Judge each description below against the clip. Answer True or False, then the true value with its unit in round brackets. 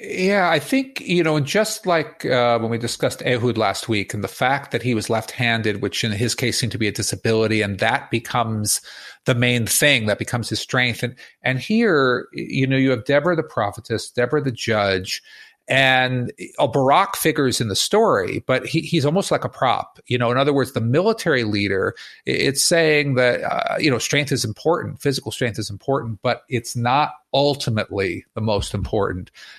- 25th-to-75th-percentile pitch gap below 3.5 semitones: False (3.9 semitones)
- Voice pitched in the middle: False (125 Hz)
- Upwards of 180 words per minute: True (195 wpm)